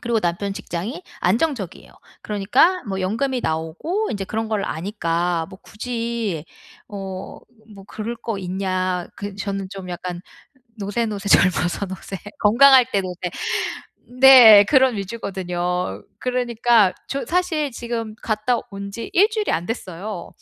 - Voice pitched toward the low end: No, high, 205 Hz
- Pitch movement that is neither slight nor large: Yes, average, 4.3 semitones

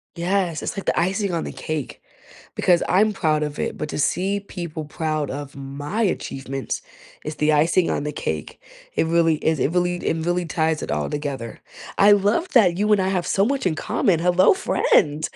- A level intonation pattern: No, average, 4.2 semitones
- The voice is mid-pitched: Yes, medium, 170 Hz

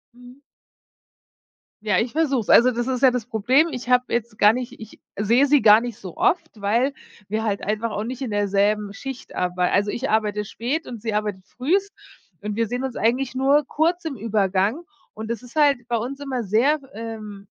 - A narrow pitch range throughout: No, average, 3.9 semitones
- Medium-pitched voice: No, high, 235 Hz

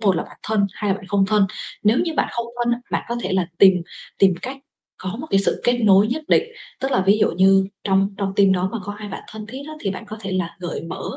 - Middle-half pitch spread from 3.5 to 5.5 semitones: No, narrow, 2.4 semitones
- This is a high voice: Yes, high, 200 Hz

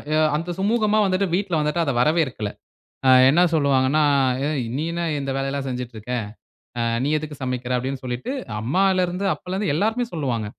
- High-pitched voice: No, medium, 150 Hz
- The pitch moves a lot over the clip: Yes, wide, 5.7 semitones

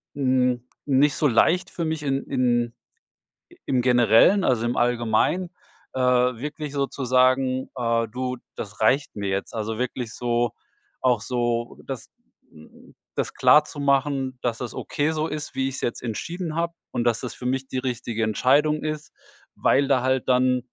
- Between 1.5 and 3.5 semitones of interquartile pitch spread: Yes, average, 2.9 semitones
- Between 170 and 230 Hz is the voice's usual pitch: No, low, 130 Hz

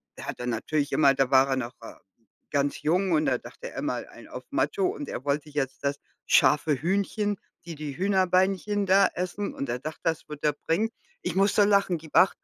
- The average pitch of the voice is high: No, medium, 160 Hz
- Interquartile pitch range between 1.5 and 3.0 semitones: No, wide, 5.6 semitones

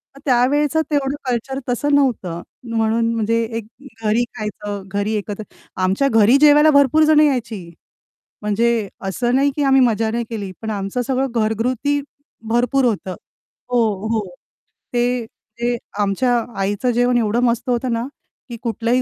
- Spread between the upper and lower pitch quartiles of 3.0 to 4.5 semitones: Yes, average, 3.3 semitones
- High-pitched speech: Yes, high, 235 Hz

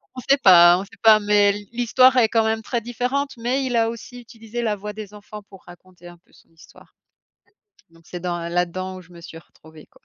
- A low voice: No, high, 210 Hz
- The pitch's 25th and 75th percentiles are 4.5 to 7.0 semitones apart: Yes, average, 4.9 semitones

